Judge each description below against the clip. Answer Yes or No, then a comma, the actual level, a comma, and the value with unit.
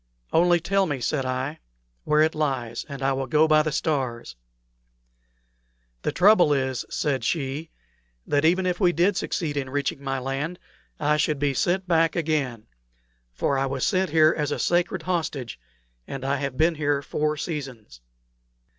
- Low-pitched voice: No, medium, 150 Hz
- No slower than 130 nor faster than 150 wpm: No, average, 165 wpm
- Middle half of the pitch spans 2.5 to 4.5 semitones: Yes, average, 3.4 semitones